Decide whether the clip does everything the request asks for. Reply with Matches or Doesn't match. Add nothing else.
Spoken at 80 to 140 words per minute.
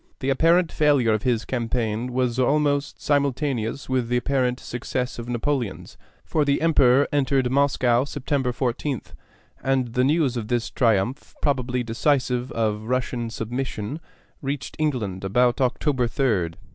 Matches